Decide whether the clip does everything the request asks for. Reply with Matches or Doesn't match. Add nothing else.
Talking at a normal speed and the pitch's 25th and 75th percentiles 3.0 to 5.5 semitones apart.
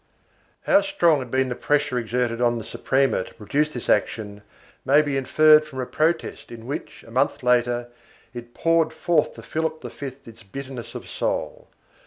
Matches